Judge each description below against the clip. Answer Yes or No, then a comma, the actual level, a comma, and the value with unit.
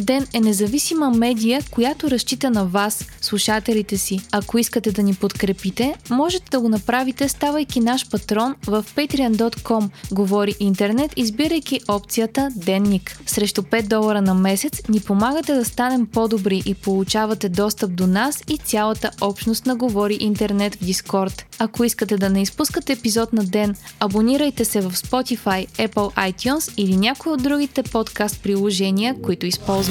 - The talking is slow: No, average, 145 wpm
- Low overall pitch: No, high, 220 Hz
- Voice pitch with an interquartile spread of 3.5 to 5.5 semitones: Yes, average, 3.9 semitones